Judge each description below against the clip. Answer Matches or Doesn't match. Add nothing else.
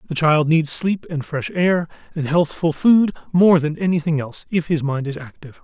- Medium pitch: Matches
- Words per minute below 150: Doesn't match